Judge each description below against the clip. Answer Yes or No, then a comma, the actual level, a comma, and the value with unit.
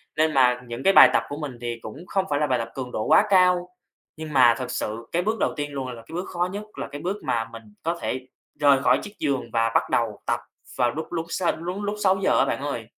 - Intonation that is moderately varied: No, wide, 6.3 semitones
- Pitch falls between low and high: Yes, medium, 145 Hz